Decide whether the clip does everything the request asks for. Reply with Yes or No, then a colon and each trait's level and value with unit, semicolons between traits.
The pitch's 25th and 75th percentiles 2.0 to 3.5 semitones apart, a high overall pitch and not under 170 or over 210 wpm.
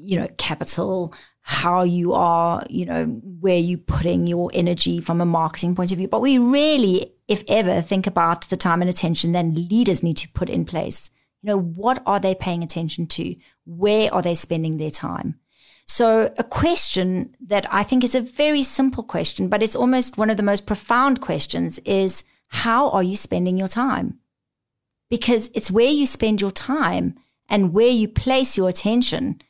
No: average, 5.3 semitones; high, 195 Hz; average, 185 wpm